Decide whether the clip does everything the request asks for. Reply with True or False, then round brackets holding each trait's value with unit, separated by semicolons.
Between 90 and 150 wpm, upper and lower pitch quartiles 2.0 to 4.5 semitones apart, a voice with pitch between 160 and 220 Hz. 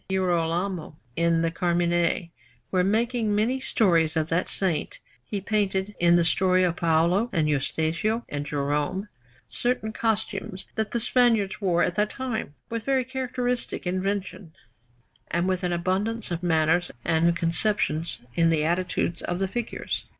True (145 wpm; 4.2 semitones; 185 Hz)